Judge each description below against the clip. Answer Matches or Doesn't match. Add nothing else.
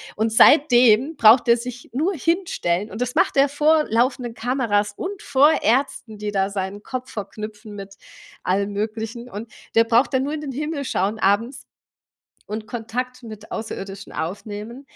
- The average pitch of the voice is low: Doesn't match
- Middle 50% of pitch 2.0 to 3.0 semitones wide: Doesn't match